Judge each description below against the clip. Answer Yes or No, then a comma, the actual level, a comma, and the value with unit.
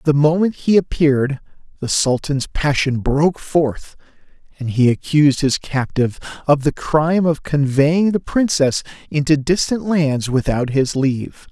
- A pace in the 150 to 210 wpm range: No, average, 140 wpm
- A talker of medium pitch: Yes, medium, 150 Hz